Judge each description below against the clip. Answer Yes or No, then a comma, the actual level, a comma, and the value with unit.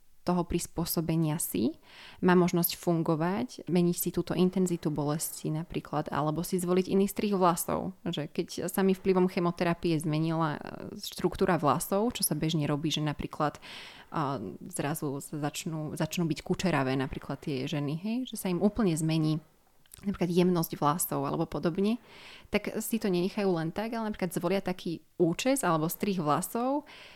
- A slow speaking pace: No, average, 150 wpm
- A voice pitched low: No, medium, 175 Hz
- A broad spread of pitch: No, average, 3.3 semitones